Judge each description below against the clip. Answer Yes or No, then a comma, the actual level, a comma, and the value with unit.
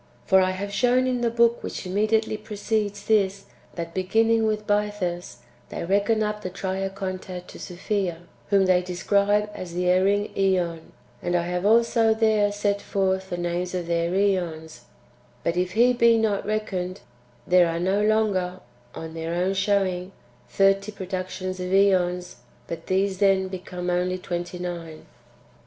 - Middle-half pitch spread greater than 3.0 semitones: No, narrow, 2.6 semitones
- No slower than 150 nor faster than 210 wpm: Yes, average, 155 wpm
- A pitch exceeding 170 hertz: Yes, high, 190 Hz